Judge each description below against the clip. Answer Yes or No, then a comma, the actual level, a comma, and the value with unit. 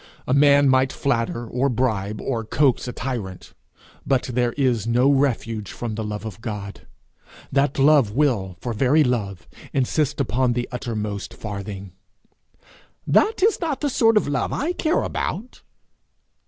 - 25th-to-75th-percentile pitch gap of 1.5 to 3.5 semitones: No, average, 4.6 semitones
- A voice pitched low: Yes, low, 125 Hz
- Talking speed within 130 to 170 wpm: Yes, average, 150 wpm